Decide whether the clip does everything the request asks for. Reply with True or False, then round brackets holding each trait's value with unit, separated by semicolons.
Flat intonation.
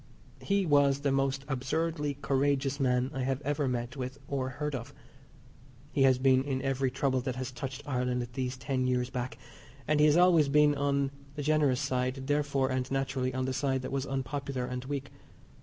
True (1.8 semitones)